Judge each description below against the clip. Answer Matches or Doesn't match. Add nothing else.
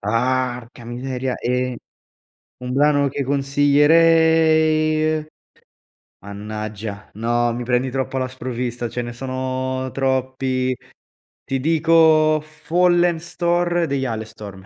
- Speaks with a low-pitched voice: Matches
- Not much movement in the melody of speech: Doesn't match